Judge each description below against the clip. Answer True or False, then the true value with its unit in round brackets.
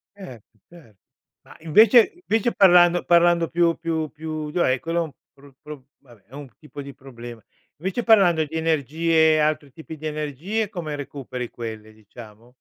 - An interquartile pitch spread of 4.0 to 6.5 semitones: True (4.5 semitones)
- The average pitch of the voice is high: False (155 Hz)